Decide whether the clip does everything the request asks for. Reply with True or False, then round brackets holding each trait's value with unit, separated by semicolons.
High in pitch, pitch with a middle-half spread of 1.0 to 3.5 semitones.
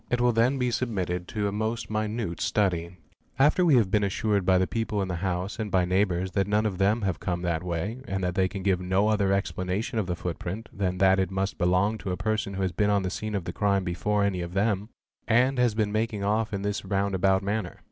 False (100 Hz; 2.8 semitones)